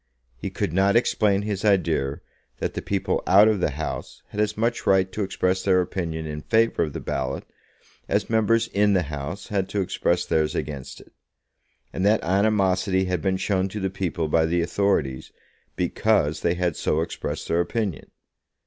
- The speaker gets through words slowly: No, average, 180 wpm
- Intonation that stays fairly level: No, average, 3.7 semitones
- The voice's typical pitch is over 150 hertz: No, very low, 95 Hz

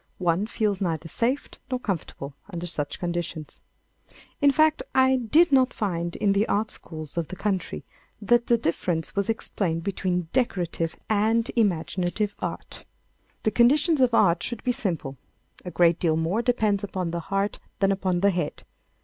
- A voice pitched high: Yes, high, 195 Hz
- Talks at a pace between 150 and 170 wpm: Yes, average, 160 wpm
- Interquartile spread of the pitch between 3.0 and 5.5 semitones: Yes, average, 5.1 semitones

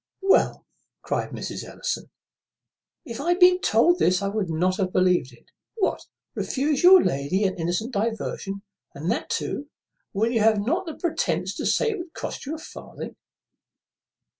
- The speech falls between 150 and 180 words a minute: Yes, average, 165 wpm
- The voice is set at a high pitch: Yes, high, 225 Hz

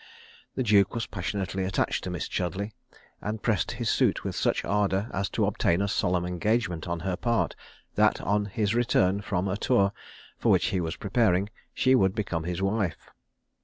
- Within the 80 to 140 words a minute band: No, average, 180 wpm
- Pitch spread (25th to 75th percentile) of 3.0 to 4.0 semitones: No, narrow, 2.6 semitones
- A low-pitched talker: Yes, low, 100 Hz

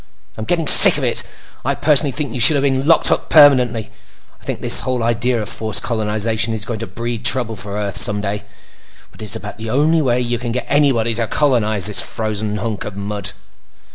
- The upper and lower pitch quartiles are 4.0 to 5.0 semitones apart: No, average, 3.3 semitones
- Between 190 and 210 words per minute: Yes, average, 200 wpm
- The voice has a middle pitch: No, low, 115 Hz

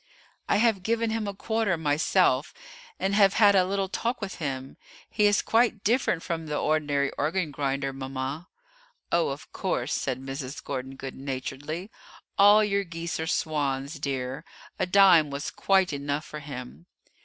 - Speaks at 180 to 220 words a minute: No, average, 160 wpm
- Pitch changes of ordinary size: No, wide, 6.2 semitones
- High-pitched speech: No, medium, 155 Hz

